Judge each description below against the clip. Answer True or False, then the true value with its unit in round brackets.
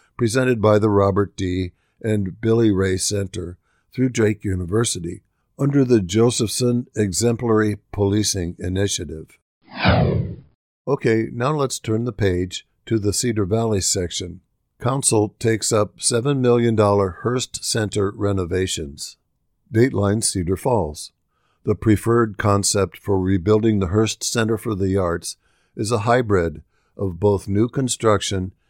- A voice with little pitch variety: False (3.4 semitones)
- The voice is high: False (105 Hz)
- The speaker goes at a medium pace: False (120 wpm)